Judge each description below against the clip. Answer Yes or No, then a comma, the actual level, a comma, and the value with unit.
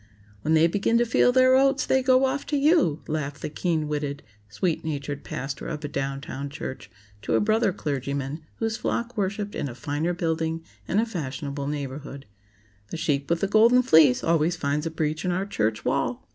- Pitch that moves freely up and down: Yes, wide, 6.6 semitones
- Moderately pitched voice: Yes, medium, 160 Hz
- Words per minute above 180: Yes, average, 195 wpm